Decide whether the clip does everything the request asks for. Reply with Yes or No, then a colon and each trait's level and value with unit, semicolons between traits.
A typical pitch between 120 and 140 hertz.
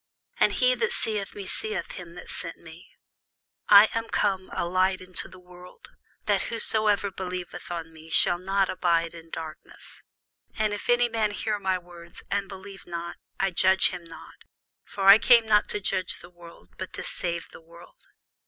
No: medium, 185 Hz